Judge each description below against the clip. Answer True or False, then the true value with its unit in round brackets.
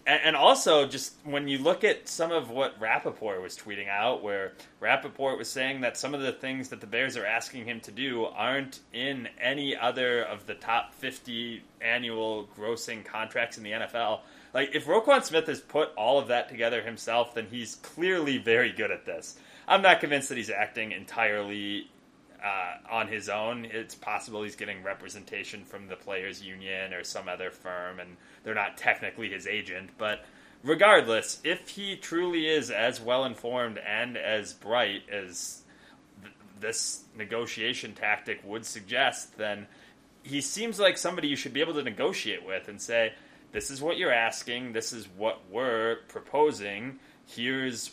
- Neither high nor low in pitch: False (120 Hz)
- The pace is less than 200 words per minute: True (170 wpm)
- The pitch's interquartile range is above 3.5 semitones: True (4.6 semitones)